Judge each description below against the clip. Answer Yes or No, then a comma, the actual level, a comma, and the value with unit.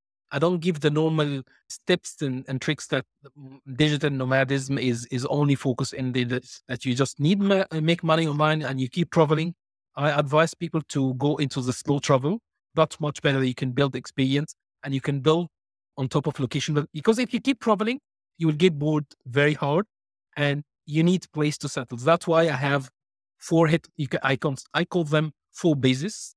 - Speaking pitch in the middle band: Yes, medium, 150 Hz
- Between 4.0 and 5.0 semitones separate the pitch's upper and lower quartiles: No, average, 3.2 semitones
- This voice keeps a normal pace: Yes, average, 190 wpm